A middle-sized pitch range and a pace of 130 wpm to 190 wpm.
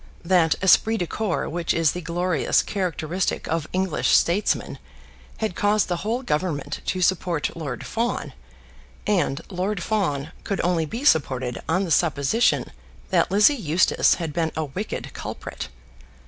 Yes: average, 3.9 semitones; average, 145 wpm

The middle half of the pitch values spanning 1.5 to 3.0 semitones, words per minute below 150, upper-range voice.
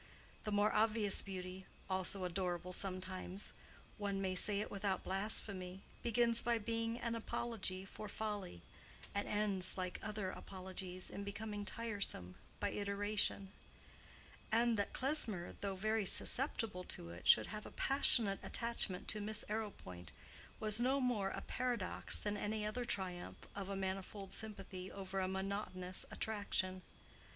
Yes: narrow, 2.5 semitones; slow, 135 wpm; high, 200 Hz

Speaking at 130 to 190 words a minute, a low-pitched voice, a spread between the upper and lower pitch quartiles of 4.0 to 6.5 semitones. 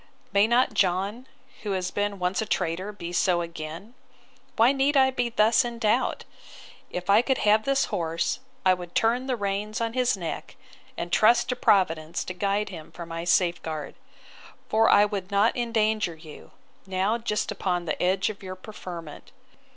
No: average, 165 wpm; high, 200 Hz; average, 4.3 semitones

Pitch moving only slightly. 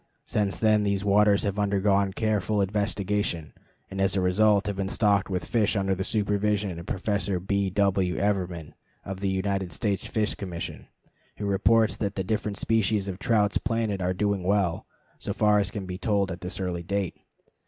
Yes: narrow, 1.6 semitones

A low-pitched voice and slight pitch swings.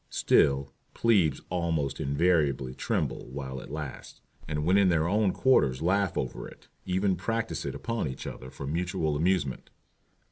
No: very low, 80 Hz; average, 5.2 semitones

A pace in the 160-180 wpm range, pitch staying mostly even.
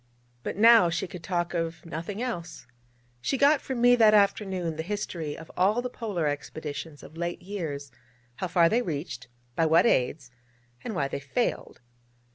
No: average, 170 wpm; average, 4.9 semitones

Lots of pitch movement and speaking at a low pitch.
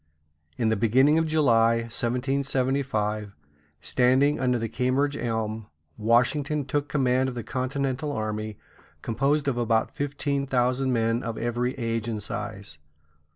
No: average, 3.3 semitones; low, 125 Hz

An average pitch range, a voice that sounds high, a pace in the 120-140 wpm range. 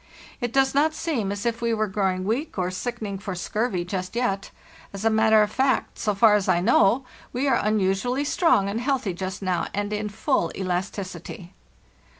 No: average, 3.9 semitones; high, 210 Hz; average, 185 wpm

